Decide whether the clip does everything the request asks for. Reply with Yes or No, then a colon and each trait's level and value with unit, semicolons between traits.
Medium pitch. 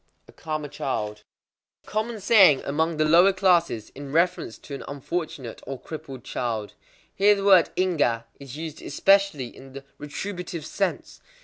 Yes: medium, 155 Hz